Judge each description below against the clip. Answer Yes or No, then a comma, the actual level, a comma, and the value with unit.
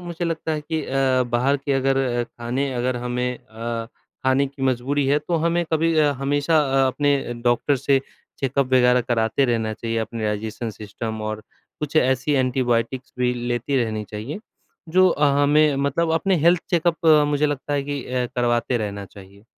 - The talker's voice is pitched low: Yes, low, 130 Hz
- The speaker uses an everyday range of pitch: Yes, average, 3.5 semitones